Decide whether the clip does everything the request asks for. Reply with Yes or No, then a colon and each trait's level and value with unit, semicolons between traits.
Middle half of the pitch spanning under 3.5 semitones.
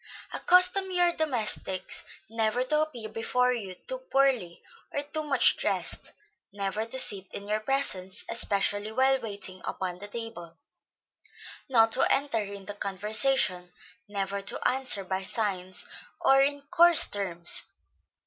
No: wide, 5.6 semitones